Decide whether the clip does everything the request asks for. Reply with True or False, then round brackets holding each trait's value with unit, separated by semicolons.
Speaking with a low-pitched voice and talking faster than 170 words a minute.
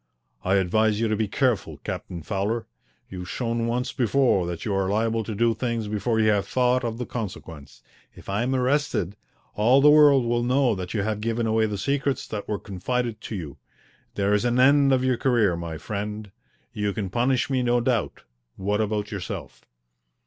True (110 Hz; 190 wpm)